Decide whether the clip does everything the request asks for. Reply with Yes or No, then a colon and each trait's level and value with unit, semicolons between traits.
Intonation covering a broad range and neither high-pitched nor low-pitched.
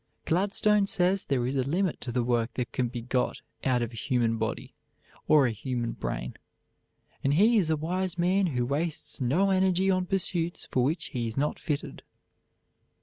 Yes: wide, 7.0 semitones; medium, 145 Hz